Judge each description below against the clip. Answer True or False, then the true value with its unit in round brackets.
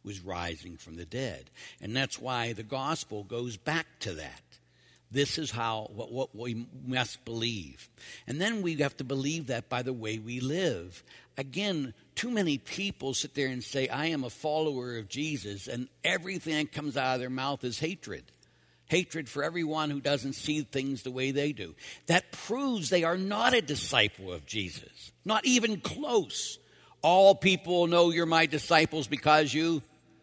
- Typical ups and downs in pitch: False (5.7 semitones)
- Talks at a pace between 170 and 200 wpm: True (175 wpm)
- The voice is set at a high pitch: False (140 Hz)